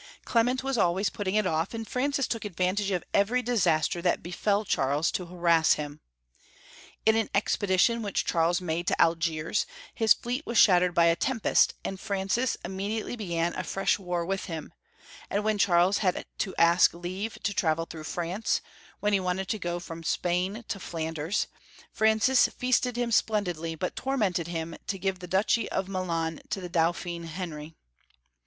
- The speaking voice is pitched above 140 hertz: Yes, medium, 185 Hz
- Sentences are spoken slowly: No, average, 175 wpm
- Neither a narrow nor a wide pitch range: Yes, average, 4.1 semitones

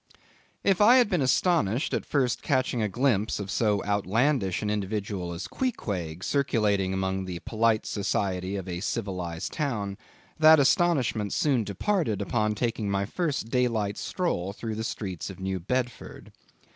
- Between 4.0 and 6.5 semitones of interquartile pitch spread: Yes, average, 5.2 semitones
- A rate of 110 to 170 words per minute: Yes, average, 150 wpm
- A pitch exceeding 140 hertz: No, low, 105 Hz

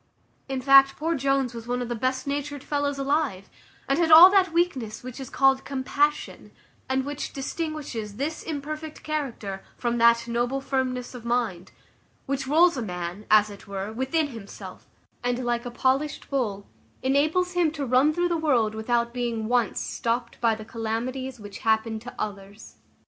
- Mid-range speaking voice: No, very high, 255 Hz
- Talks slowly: No, average, 170 wpm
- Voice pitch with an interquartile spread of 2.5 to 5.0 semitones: Yes, average, 3.9 semitones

